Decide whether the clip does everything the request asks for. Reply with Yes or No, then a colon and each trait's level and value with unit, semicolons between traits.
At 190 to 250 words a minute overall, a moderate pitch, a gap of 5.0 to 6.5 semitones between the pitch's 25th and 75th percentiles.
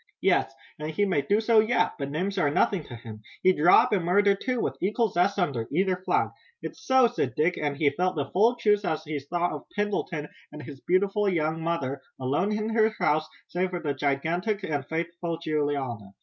Yes: fast, 205 wpm; medium, 175 Hz; wide, 5.4 semitones